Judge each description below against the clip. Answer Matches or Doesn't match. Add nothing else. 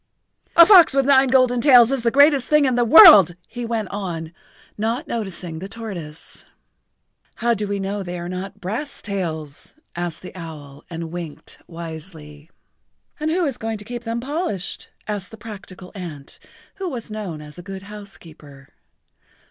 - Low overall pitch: Doesn't match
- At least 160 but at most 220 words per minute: Matches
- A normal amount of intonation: Doesn't match